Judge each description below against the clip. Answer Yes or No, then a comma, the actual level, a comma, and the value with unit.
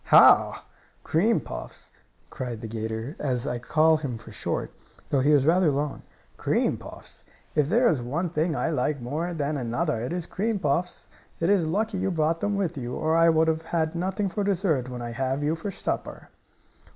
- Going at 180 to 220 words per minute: Yes, average, 190 wpm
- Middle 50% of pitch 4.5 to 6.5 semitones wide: Yes, average, 4.9 semitones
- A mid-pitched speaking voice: Yes, medium, 155 Hz